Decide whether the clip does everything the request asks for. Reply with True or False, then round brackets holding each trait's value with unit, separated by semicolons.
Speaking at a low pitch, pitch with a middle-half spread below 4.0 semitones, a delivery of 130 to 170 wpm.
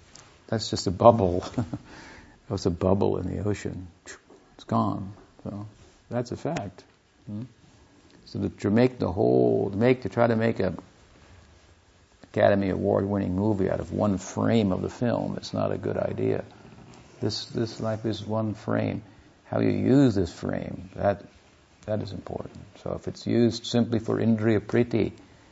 True (100 Hz; 3.4 semitones; 165 wpm)